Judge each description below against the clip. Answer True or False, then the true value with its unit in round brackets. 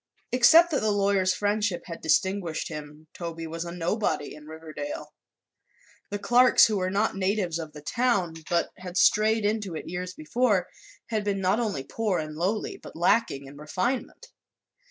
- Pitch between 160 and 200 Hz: True (185 Hz)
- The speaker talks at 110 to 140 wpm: False (165 wpm)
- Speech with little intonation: False (4.7 semitones)